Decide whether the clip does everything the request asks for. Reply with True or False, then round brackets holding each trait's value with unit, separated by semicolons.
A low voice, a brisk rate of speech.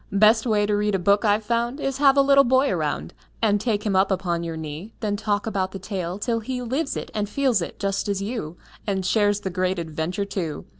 False (205 Hz; 235 wpm)